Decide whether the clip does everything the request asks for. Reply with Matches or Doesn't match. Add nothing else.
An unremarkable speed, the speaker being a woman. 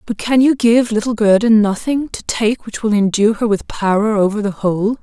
Doesn't match